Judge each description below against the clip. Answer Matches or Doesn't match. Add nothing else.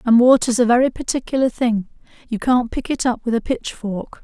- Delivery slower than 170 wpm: Doesn't match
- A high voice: Matches